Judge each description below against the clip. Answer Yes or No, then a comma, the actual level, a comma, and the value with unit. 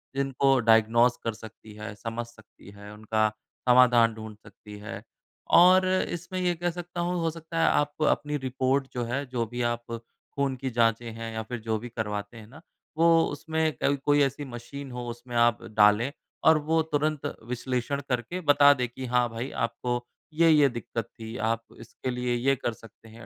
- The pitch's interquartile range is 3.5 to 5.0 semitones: Yes, average, 3.9 semitones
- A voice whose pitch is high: No, low, 120 Hz